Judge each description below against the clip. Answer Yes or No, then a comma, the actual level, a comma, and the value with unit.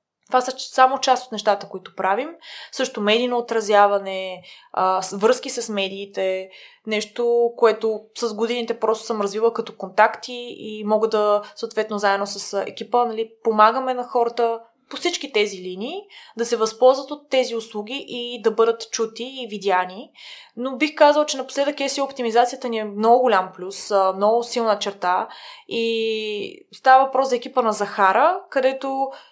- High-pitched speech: Yes, high, 230 Hz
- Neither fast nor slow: Yes, average, 150 wpm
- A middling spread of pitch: Yes, average, 3.6 semitones